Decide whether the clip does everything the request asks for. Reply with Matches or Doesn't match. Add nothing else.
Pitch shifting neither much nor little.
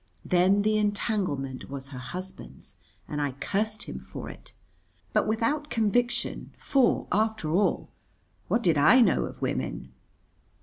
Doesn't match